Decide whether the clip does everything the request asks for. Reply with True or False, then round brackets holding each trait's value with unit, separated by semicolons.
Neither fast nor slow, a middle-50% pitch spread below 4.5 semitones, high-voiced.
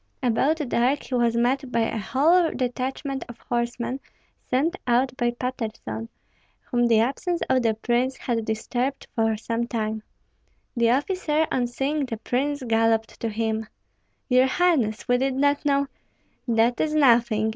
True (155 wpm; 2.9 semitones; 245 Hz)